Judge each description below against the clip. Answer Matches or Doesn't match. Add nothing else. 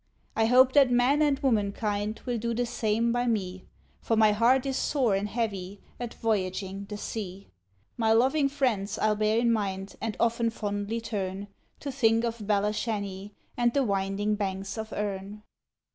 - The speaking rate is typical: Matches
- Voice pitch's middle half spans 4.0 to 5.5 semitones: Doesn't match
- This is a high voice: Matches